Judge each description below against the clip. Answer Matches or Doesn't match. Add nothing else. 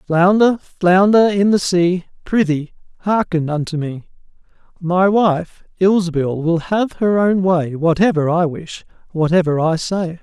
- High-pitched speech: Doesn't match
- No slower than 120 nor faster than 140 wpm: Matches